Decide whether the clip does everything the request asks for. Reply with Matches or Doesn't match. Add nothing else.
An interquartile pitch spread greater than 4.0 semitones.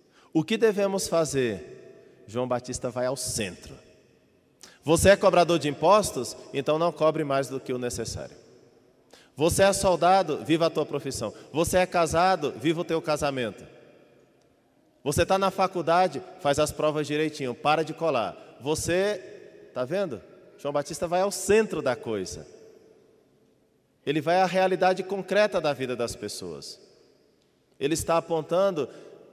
Matches